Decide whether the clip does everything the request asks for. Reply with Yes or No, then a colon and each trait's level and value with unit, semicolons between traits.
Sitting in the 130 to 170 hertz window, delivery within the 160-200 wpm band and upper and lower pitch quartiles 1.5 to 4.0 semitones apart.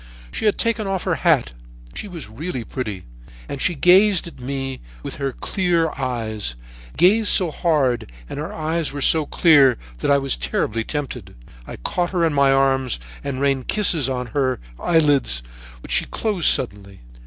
No: medium, 140 Hz; average, 170 wpm; average, 5.1 semitones